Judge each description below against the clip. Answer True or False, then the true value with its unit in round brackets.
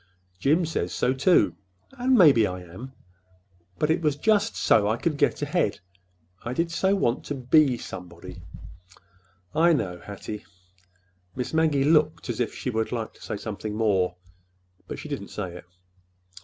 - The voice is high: False (125 Hz)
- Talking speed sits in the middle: True (160 wpm)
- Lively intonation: True (8.7 semitones)